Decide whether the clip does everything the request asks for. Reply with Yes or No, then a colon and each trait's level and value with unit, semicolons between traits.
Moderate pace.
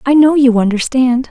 Yes: average, 185 wpm